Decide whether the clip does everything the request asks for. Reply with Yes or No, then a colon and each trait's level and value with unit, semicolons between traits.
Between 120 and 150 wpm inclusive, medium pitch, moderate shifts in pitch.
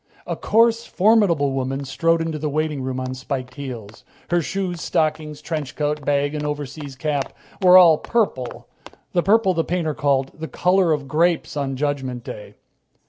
No: average, 165 wpm; medium, 150 Hz; average, 3.9 semitones